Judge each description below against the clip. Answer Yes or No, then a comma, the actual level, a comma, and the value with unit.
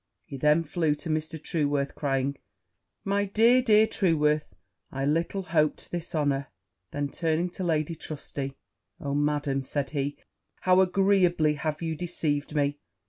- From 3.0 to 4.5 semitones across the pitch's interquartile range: Yes, average, 3.3 semitones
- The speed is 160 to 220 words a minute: No, average, 140 wpm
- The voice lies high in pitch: No, medium, 155 Hz